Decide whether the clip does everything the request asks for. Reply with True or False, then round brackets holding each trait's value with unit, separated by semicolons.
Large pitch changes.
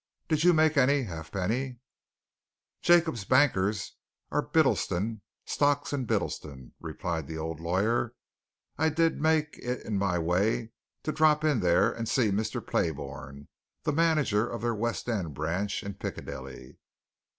True (8.2 semitones)